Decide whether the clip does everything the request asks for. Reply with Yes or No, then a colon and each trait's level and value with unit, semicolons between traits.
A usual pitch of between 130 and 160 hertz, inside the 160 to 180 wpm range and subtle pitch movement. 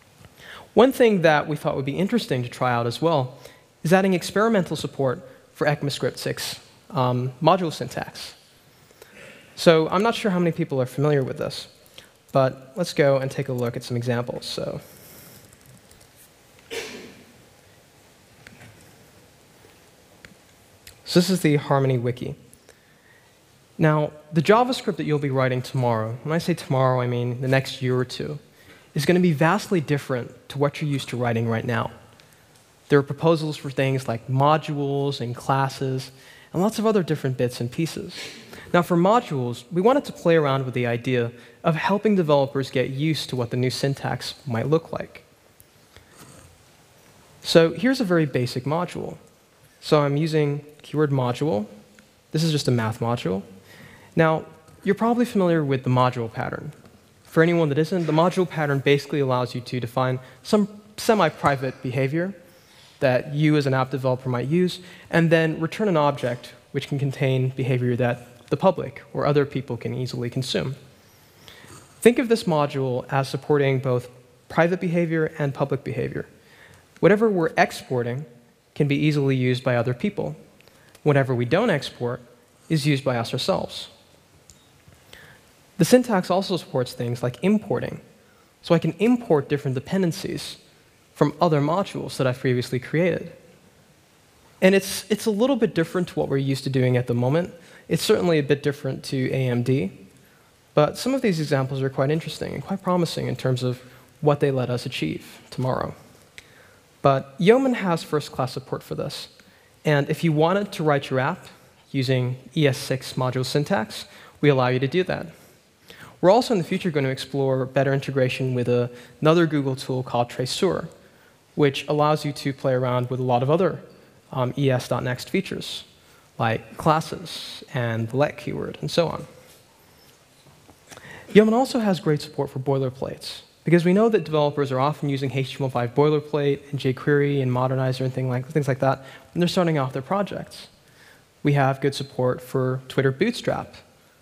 No: medium, 140 Hz; average, 165 wpm; average, 4.4 semitones